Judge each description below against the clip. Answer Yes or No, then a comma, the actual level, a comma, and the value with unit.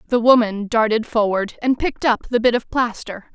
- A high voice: Yes, high, 230 Hz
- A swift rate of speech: No, average, 195 wpm